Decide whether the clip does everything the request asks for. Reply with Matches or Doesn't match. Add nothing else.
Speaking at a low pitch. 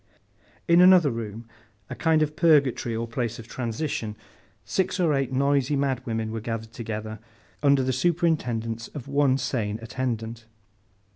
Matches